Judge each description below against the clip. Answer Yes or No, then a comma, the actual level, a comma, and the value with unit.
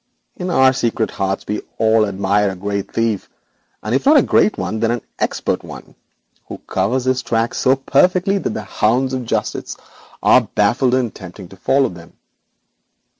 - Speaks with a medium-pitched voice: No, low, 115 Hz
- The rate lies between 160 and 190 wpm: Yes, average, 175 wpm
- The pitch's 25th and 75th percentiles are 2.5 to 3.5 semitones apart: No, average, 4.4 semitones